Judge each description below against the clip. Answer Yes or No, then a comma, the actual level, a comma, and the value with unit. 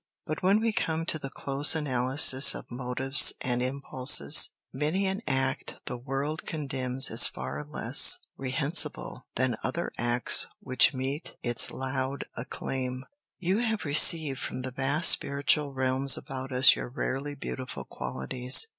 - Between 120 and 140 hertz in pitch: Yes, low, 135 Hz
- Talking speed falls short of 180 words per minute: Yes, average, 140 wpm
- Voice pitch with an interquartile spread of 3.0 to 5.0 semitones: No, narrow, 2.5 semitones